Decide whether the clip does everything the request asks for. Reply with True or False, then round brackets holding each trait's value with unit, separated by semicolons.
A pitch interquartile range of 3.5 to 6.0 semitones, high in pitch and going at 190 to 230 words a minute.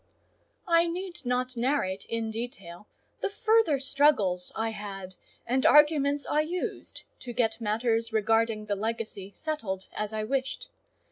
False (5.3 semitones; 230 Hz; 135 wpm)